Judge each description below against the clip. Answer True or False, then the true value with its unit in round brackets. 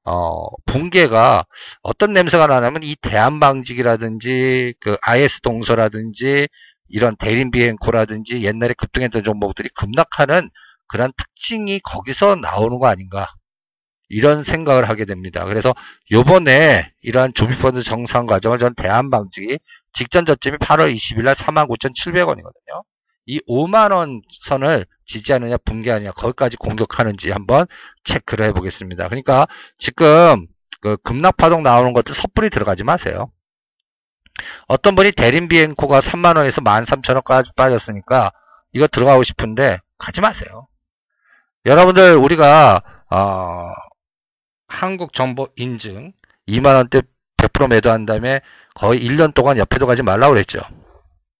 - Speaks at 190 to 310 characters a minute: True (295 characters per minute)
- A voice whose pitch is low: True (125 Hz)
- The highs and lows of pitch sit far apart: False (4.5 semitones)